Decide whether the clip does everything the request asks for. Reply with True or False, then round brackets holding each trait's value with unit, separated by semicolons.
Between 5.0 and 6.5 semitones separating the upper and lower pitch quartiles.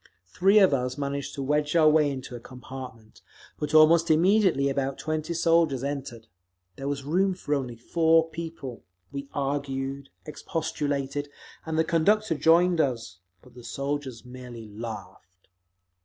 False (4.0 semitones)